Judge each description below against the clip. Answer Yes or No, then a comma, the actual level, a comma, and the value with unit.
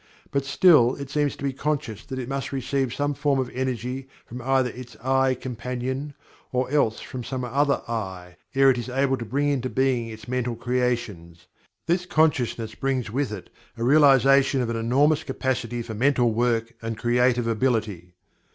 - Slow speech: No, average, 175 wpm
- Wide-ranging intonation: No, average, 2.7 semitones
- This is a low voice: Yes, low, 125 Hz